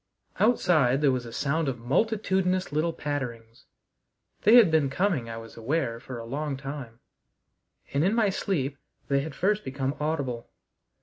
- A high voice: No, medium, 140 Hz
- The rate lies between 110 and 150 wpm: No, average, 160 wpm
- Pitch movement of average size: No, wide, 5.7 semitones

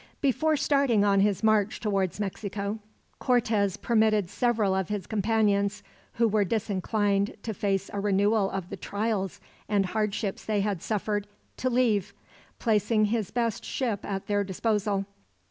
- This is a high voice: Yes, high, 210 Hz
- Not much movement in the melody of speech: Yes, narrow, 1.9 semitones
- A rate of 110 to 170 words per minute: Yes, average, 145 wpm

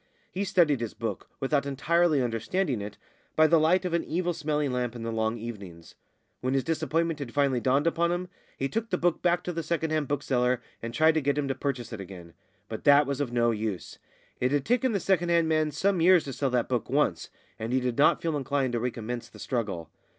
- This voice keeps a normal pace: No, fast, 230 wpm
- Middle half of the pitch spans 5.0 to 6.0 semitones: Yes, wide, 5.5 semitones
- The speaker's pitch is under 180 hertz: Yes, medium, 140 Hz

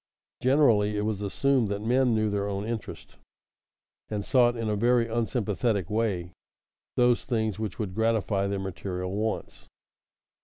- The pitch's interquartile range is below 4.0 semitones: Yes, narrow, 2.6 semitones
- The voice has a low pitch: Yes, low, 110 Hz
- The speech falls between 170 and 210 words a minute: No, average, 145 wpm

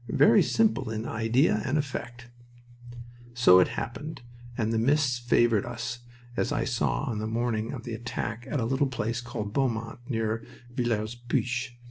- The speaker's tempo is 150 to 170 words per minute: Yes, average, 160 wpm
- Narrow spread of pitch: Yes, narrow, 2.0 semitones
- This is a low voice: Yes, low, 120 Hz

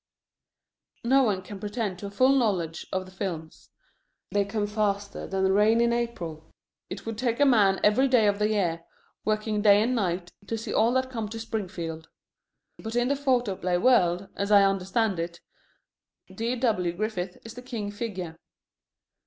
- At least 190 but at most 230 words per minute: No, average, 170 wpm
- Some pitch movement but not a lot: Yes, average, 3.7 semitones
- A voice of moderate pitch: No, high, 210 Hz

